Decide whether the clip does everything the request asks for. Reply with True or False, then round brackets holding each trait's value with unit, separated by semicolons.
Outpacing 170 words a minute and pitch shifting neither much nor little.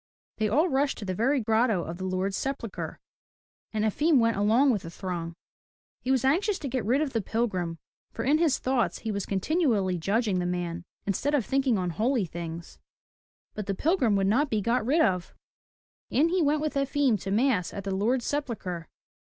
False (195 wpm; 6.2 semitones)